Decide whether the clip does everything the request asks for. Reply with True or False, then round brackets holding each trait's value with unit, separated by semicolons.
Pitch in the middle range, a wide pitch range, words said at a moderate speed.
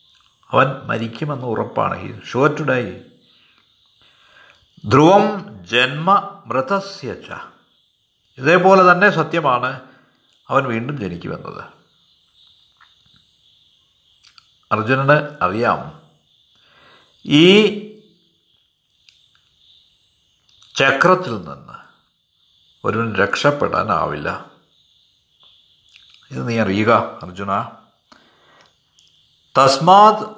False (145 Hz; 8.1 semitones; 55 wpm)